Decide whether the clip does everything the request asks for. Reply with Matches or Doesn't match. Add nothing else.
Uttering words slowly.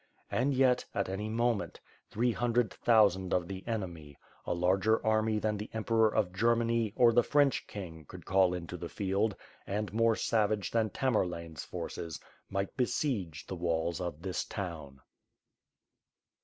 Doesn't match